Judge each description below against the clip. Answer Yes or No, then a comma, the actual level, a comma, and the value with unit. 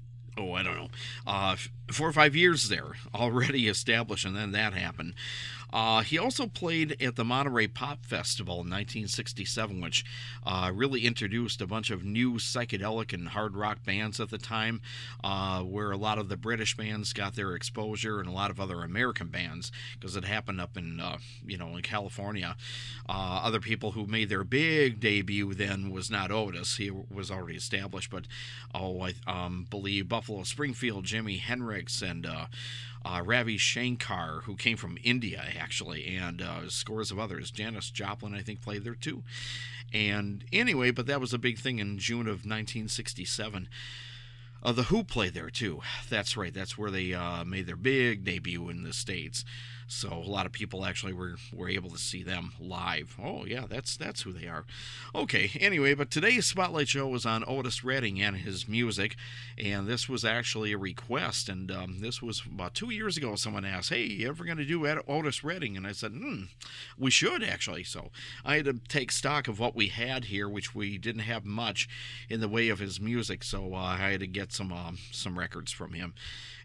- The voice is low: Yes, low, 110 Hz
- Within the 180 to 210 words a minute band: Yes, average, 195 wpm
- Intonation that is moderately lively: Yes, average, 3.6 semitones